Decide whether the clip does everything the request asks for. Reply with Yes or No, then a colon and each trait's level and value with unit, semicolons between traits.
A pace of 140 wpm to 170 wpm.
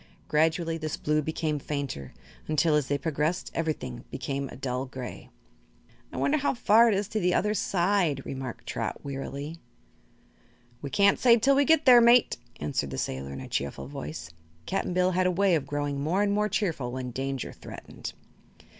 No: average, 180 wpm